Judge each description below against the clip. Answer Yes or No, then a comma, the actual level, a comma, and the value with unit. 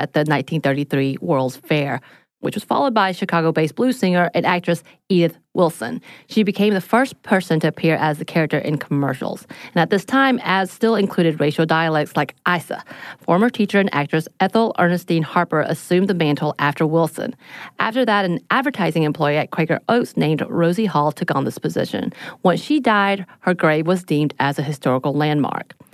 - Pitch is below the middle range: No, medium, 165 Hz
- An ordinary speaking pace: Yes, average, 180 wpm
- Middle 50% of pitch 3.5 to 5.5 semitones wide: Yes, average, 4.1 semitones